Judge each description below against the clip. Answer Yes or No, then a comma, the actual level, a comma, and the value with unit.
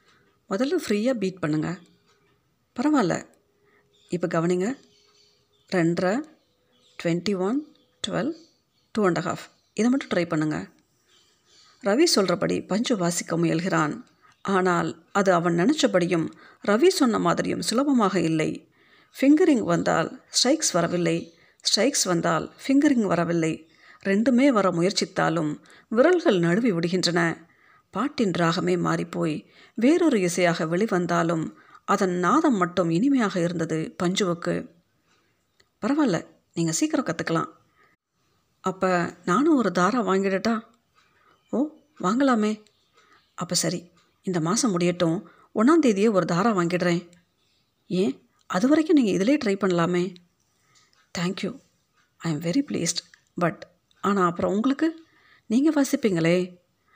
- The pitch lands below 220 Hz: Yes, high, 190 Hz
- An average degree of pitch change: No, wide, 6.9 semitones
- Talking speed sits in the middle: Yes, average, 100 wpm